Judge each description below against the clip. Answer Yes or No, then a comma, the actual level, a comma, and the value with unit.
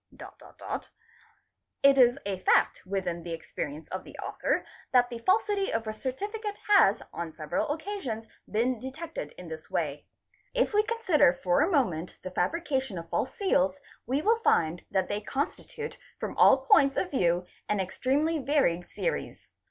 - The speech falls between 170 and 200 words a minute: No, average, 160 wpm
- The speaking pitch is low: No, high, 245 Hz